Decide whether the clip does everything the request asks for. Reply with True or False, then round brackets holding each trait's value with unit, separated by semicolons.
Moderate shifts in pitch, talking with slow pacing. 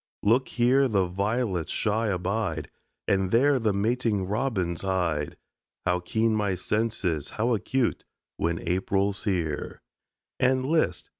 True (4.2 semitones; 125 wpm)